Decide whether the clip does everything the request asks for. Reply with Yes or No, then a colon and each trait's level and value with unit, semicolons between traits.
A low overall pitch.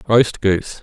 Yes: low, 105 Hz